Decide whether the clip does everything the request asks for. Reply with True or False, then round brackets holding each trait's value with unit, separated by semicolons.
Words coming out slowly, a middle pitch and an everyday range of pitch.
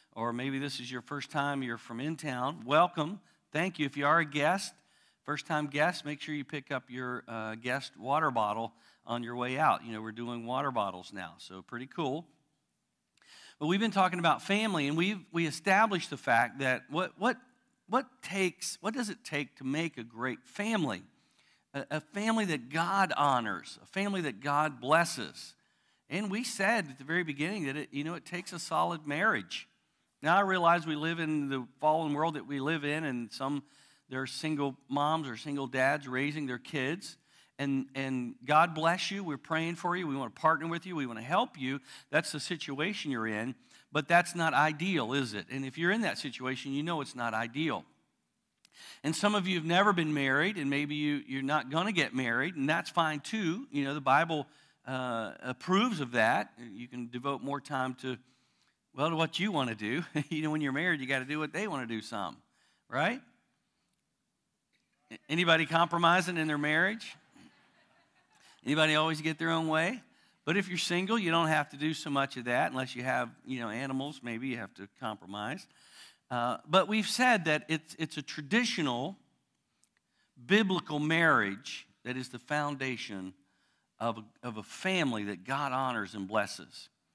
False (195 wpm; 150 Hz; 4.5 semitones)